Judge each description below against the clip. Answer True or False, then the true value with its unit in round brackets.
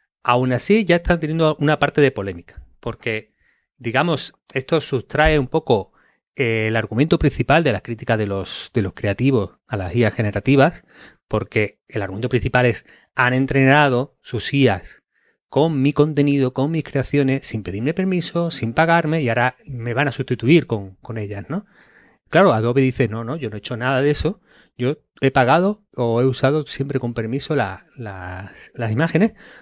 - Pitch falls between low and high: False (130 Hz)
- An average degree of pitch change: True (4.7 semitones)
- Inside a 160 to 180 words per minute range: True (175 wpm)